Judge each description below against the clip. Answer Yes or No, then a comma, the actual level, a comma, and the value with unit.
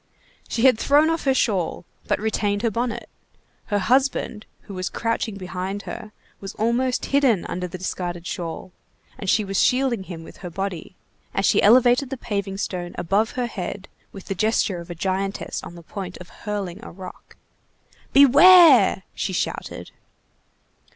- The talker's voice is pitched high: Yes, high, 200 Hz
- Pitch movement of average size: Yes, average, 4.6 semitones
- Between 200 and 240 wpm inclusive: No, average, 165 wpm